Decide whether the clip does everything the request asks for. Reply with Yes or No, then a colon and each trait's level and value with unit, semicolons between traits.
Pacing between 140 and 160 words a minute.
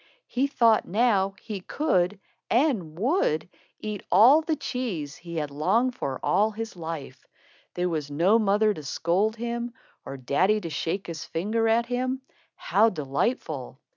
Yes: average, 150 wpm